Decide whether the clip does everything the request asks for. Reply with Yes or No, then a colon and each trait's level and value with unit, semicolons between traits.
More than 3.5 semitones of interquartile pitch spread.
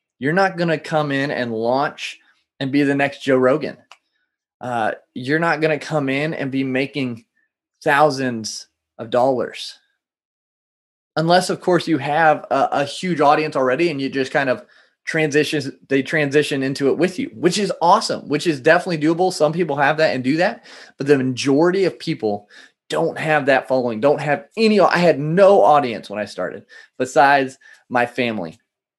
No: average, 3.2 semitones